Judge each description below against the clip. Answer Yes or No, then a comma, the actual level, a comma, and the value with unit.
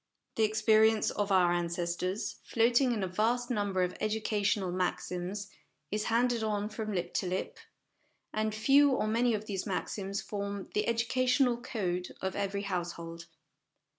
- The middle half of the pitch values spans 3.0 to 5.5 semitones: Yes, average, 3.3 semitones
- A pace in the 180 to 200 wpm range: No, average, 145 wpm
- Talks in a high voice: Yes, high, 210 Hz